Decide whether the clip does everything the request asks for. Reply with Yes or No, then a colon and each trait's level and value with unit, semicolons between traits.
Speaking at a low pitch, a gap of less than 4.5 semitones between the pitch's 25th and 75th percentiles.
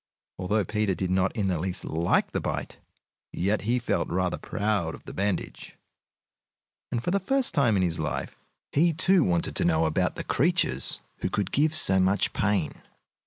No: low, 100 Hz; wide, 5.4 semitones